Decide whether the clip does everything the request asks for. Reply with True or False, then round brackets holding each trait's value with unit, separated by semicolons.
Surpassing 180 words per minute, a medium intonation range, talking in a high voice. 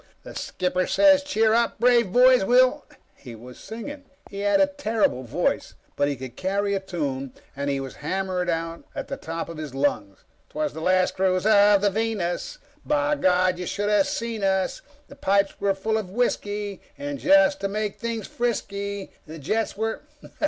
True (190 wpm; 4.8 semitones; 200 Hz)